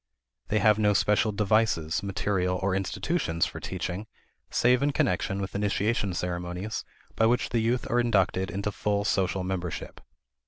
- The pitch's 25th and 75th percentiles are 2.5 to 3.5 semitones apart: Yes, average, 2.9 semitones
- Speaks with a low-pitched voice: Yes, low, 100 Hz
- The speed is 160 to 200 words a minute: No, average, 150 wpm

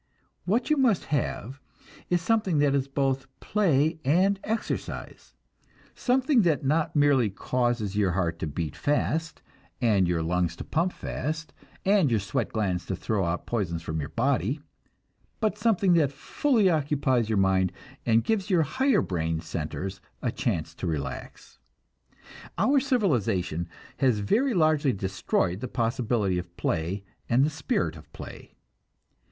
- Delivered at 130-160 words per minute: Yes, average, 145 wpm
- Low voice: Yes, low, 130 Hz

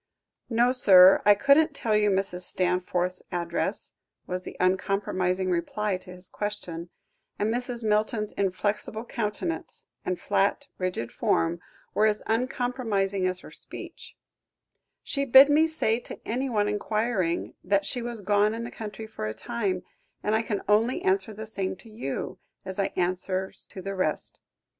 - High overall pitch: Yes, high, 205 Hz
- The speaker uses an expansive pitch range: No, average, 3.8 semitones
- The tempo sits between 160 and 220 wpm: No, average, 150 wpm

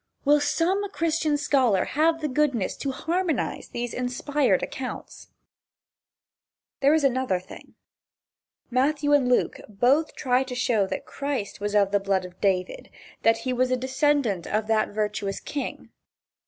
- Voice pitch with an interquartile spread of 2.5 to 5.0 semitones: No, wide, 5.6 semitones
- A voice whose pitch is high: Yes, very high, 255 Hz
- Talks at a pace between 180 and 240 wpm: No, average, 145 wpm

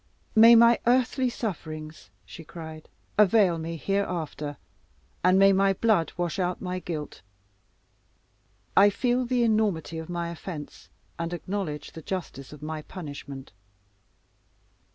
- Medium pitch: Yes, medium, 180 Hz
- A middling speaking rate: No, slow, 130 wpm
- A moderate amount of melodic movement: Yes, average, 4.5 semitones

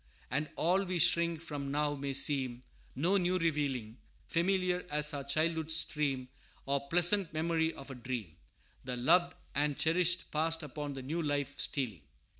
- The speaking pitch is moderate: Yes, medium, 150 Hz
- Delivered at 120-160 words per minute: Yes, average, 155 wpm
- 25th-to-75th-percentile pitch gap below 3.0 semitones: No, average, 3.5 semitones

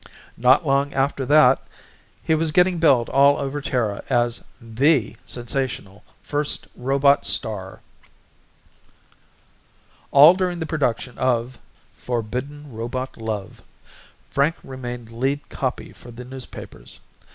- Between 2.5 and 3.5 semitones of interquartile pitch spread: Yes, average, 3.2 semitones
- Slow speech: Yes, slow, 110 wpm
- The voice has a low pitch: Yes, low, 130 Hz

